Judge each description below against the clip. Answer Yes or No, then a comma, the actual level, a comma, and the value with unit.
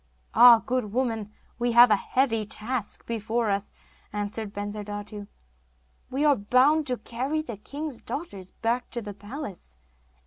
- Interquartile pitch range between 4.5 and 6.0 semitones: No, average, 3.6 semitones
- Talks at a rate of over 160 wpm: No, average, 140 wpm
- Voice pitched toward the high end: Yes, high, 230 Hz